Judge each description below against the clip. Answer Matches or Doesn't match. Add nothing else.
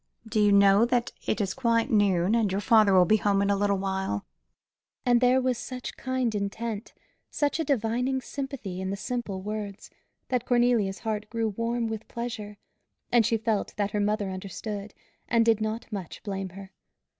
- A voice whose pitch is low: Doesn't match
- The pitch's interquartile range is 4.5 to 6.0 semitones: Doesn't match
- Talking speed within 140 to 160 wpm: Doesn't match